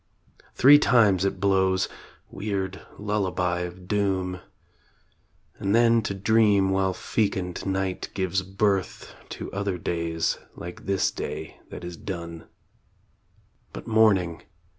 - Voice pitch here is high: No, very low, 95 Hz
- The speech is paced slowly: Yes, slow, 115 wpm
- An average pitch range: No, narrow, 1.9 semitones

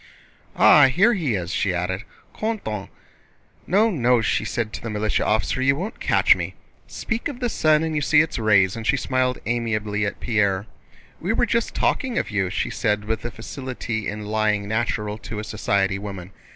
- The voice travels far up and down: Yes, wide, 5.9 semitones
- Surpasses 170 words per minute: Yes, average, 190 wpm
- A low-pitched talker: Yes, low, 110 Hz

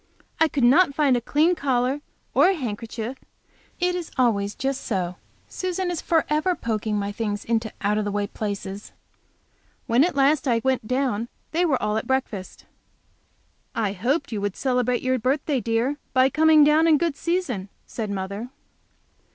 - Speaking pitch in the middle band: No, very high, 255 Hz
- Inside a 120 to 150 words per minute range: No, average, 165 wpm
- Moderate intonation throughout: No, wide, 5.8 semitones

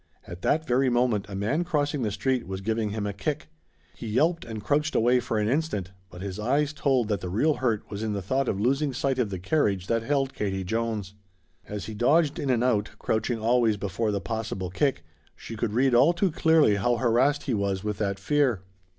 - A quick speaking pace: Yes, fast, 220 wpm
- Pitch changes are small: No, average, 5.0 semitones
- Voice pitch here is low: Yes, low, 115 Hz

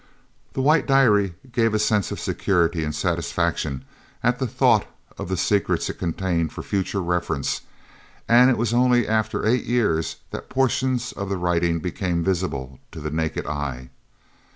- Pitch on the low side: Yes, very low, 95 Hz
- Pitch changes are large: Yes, wide, 6.3 semitones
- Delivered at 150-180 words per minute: Yes, average, 160 wpm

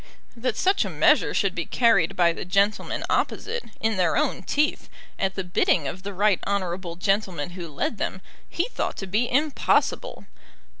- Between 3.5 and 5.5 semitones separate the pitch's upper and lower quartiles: Yes, average, 4.5 semitones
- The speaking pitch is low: No, high, 195 Hz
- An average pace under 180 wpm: Yes, average, 170 wpm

